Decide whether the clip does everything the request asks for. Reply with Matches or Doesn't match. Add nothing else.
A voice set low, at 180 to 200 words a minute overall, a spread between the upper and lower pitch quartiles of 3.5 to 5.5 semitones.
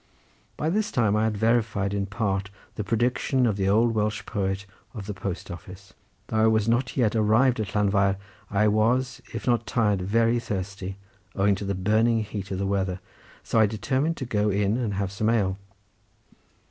Doesn't match